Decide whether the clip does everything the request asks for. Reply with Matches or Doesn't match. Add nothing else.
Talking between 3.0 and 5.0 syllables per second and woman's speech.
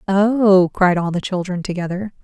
Matches